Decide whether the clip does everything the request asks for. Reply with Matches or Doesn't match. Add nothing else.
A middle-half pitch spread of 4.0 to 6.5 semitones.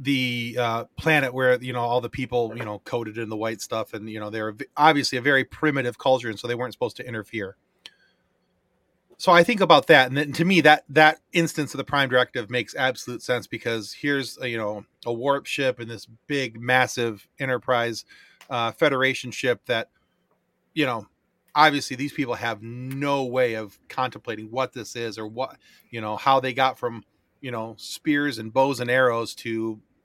Doesn't match